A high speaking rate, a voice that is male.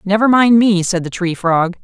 No: fast, 230 wpm; female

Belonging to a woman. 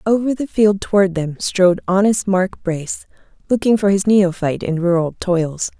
Yes: female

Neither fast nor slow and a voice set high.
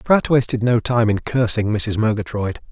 No: average, 175 wpm; low, 115 Hz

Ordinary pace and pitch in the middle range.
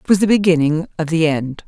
No: fast, 250 wpm; medium, 170 Hz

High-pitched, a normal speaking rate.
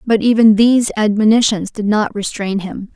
Yes: high, 215 Hz; average, 160 wpm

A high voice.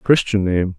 No: low, 100 Hz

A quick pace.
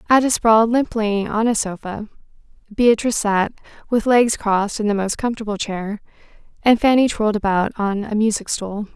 No: average, 160 wpm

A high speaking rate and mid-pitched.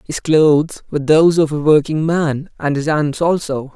No: average, 190 wpm; medium, 150 Hz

